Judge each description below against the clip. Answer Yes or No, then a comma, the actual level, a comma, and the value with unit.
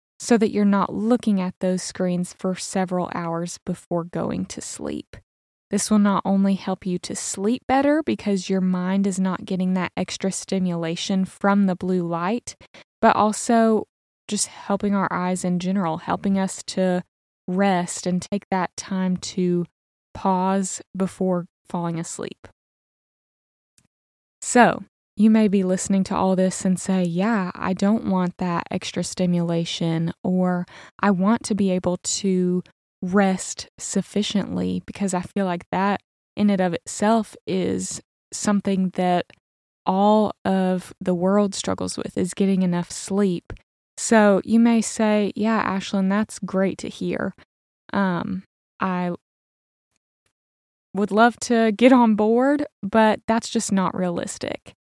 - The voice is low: No, high, 190 Hz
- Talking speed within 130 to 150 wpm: Yes, average, 140 wpm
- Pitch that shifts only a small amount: Yes, narrow, 2.3 semitones